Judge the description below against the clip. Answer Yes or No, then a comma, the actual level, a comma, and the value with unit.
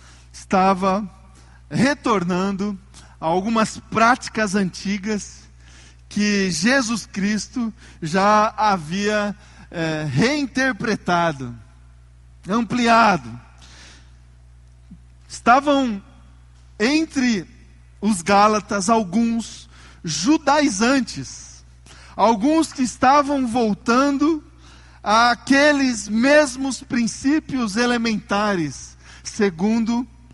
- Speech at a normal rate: No, slow, 55 wpm